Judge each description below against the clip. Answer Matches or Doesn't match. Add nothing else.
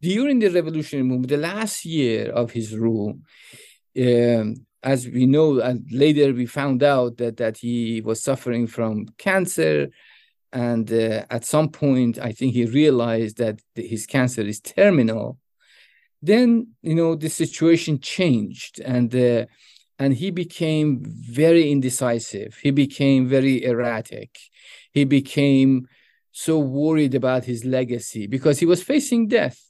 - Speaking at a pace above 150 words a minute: Doesn't match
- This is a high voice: Doesn't match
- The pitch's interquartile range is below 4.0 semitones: Doesn't match